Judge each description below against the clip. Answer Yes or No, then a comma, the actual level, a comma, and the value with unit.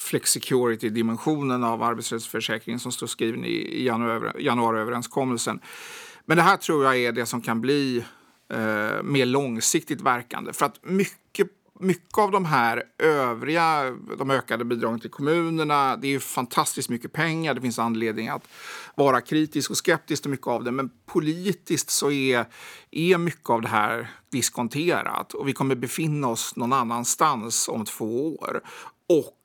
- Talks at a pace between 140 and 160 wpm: Yes, average, 150 wpm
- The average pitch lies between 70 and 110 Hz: No, low, 125 Hz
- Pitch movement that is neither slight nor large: Yes, average, 4.2 semitones